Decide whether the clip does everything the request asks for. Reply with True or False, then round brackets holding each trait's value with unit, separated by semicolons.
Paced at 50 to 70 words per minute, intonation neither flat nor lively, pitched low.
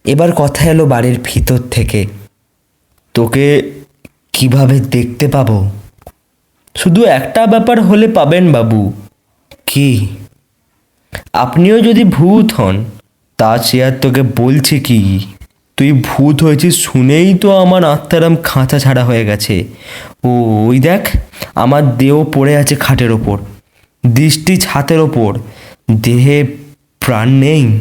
False (110 wpm; 4.8 semitones; 130 Hz)